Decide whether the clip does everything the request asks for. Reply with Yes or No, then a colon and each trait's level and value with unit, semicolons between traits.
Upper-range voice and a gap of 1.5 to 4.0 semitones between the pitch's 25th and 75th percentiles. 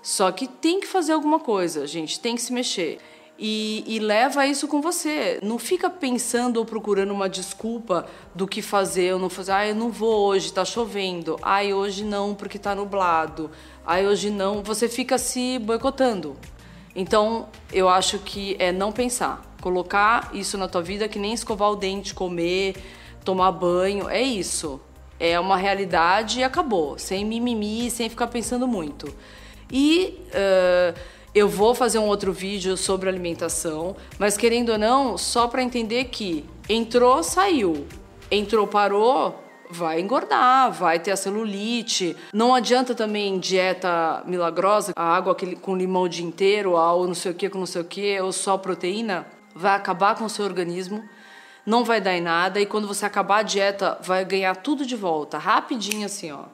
Yes: high, 200 Hz; average, 3.7 semitones